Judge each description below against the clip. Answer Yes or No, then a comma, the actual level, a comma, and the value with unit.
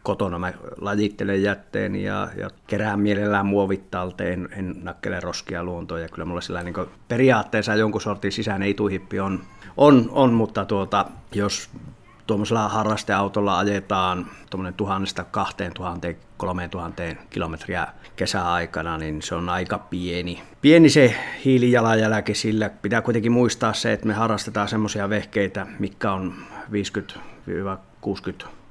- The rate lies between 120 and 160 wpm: Yes, average, 130 wpm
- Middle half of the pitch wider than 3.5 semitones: No, average, 2.8 semitones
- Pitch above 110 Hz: No, low, 100 Hz